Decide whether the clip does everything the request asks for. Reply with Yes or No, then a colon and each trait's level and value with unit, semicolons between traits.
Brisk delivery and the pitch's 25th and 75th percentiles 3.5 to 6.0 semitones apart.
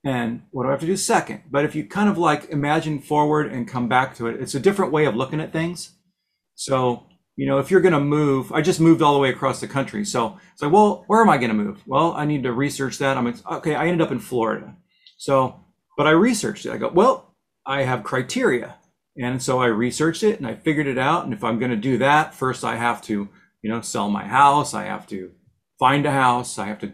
Yes: fast, 255 wpm; average, 3.9 semitones